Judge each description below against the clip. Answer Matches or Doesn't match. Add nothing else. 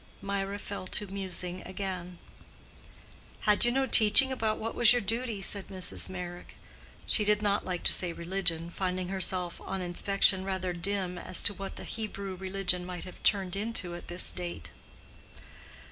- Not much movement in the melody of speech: Matches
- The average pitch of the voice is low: Doesn't match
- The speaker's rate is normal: Matches